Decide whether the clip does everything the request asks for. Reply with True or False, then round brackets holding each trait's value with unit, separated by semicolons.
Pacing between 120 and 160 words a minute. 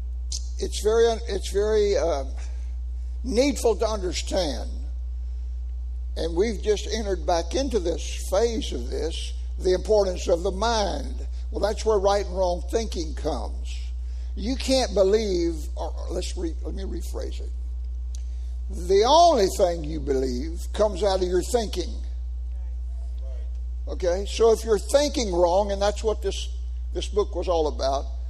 True (140 wpm)